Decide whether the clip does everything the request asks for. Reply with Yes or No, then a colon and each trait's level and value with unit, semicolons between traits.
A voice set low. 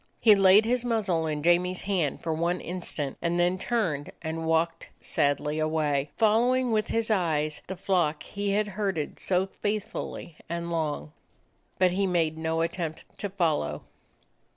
No: medium, 175 Hz